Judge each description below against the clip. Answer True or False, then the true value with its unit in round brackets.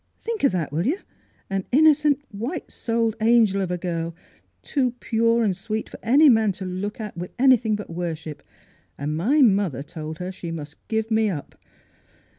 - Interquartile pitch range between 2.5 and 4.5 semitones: False (5.3 semitones)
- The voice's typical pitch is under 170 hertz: False (210 Hz)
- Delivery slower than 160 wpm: False (180 wpm)